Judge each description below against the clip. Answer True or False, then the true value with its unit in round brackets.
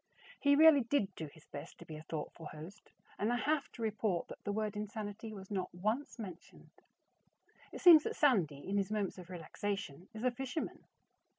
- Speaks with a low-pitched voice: False (205 Hz)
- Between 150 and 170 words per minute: False (190 wpm)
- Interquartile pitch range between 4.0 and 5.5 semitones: True (5.0 semitones)